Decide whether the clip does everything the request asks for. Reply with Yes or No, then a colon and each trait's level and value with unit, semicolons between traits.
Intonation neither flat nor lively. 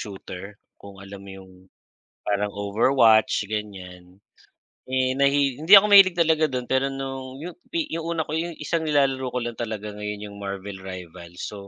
No: wide, 6.3 semitones